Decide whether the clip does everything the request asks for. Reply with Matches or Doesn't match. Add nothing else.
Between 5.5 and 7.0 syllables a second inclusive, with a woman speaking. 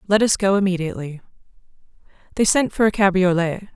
Matches